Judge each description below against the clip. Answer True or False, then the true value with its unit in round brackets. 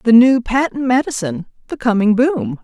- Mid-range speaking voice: False (235 Hz)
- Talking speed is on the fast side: False (135 wpm)